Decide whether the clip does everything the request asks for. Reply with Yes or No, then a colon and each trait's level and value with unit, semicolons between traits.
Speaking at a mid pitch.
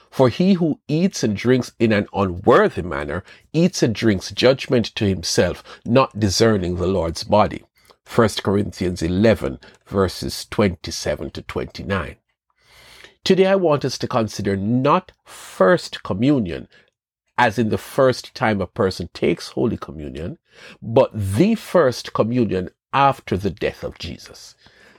No: low, 110 Hz